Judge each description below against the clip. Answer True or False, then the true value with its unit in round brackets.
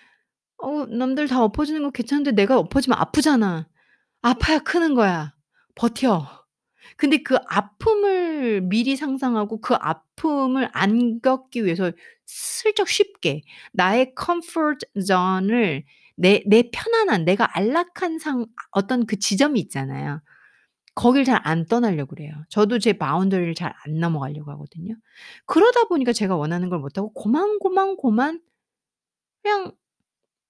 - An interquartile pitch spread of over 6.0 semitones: True (8.0 semitones)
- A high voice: True (235 Hz)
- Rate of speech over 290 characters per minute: False (270 characters per minute)